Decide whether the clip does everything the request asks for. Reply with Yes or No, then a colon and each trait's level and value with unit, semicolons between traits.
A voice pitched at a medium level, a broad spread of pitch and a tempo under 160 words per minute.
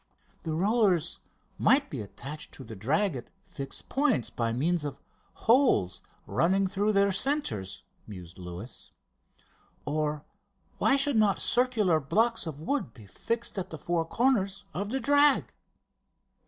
Yes: medium, 180 Hz; wide, 9.0 semitones; average, 140 wpm